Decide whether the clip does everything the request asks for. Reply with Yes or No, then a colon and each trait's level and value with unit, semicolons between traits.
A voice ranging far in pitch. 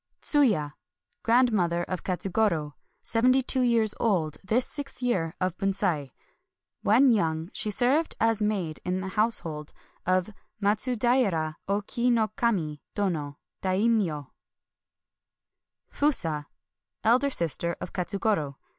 Yes: wide, 5.7 semitones